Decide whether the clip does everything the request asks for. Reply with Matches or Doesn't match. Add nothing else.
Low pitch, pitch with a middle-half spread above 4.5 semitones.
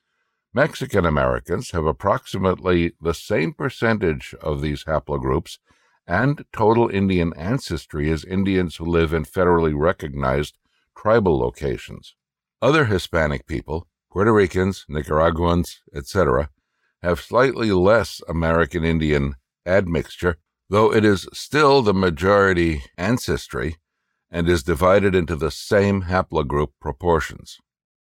Doesn't match